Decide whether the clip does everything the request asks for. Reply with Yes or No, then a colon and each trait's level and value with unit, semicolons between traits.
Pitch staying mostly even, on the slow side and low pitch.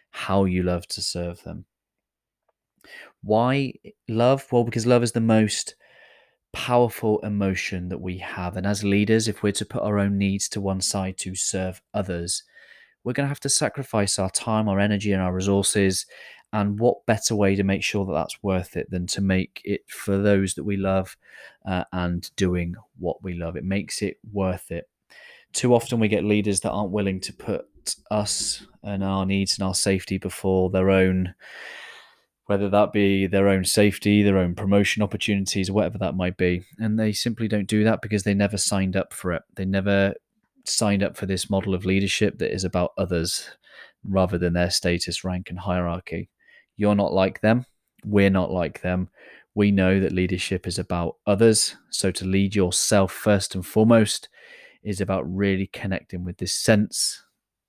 No: narrow, 2.0 semitones; average, 180 wpm; low, 100 Hz